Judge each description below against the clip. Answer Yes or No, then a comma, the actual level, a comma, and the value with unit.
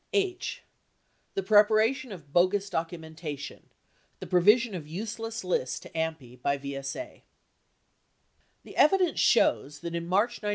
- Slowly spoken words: Yes, slow, 125 wpm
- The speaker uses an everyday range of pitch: No, wide, 6.1 semitones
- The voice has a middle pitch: Yes, medium, 180 Hz